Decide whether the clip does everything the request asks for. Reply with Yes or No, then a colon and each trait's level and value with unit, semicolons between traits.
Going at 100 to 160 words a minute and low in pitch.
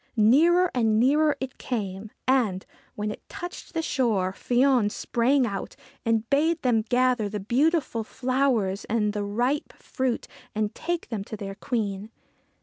No: average, 145 wpm; high, 235 Hz